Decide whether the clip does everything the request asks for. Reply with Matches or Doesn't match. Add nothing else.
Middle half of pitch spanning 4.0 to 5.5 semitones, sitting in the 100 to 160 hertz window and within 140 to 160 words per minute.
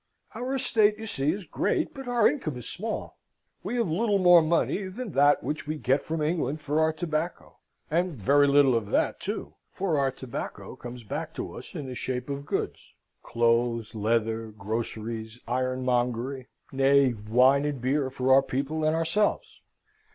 Doesn't match